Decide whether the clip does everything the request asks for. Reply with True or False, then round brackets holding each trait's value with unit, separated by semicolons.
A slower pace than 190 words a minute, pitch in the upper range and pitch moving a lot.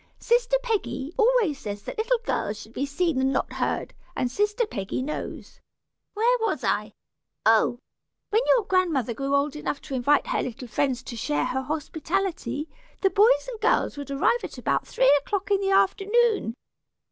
True (170 wpm; 315 Hz; 8.5 semitones)